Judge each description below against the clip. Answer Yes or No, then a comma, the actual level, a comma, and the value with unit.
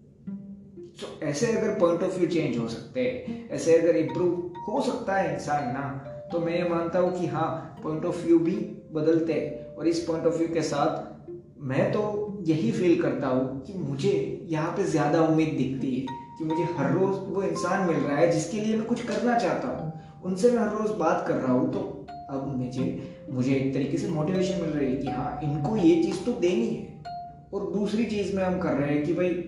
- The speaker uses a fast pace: Yes, fast, 215 wpm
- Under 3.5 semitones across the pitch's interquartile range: No, average, 4.1 semitones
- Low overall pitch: No, medium, 170 Hz